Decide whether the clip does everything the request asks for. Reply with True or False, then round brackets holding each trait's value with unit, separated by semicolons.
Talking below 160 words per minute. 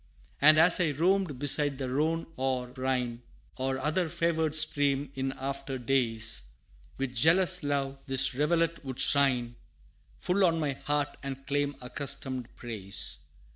True (135 wpm)